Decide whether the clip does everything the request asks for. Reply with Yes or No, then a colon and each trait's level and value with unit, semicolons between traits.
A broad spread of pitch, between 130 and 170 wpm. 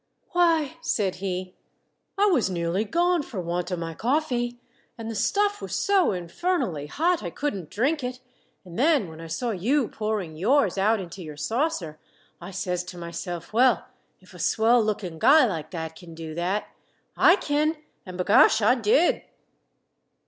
Yes: wide, 8.2 semitones; average, 165 wpm